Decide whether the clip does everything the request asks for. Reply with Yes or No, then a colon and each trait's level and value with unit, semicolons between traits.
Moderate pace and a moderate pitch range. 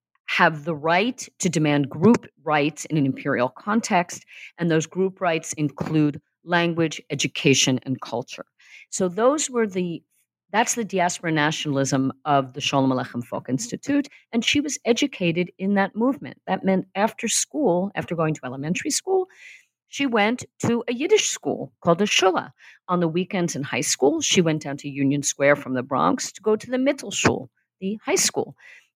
No: average, 170 wpm; wide, 6.7 semitones